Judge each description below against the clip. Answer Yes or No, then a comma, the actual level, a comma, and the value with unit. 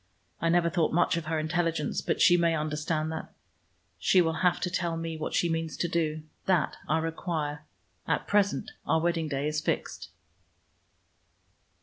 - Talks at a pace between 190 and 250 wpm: No, average, 170 wpm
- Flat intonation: Yes, narrow, 1.8 semitones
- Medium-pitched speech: Yes, medium, 165 Hz